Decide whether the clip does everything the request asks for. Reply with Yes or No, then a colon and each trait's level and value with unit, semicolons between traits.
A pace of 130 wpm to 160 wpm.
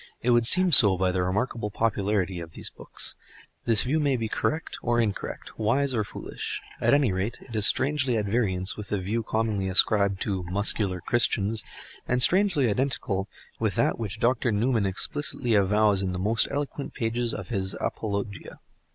No: average, 175 wpm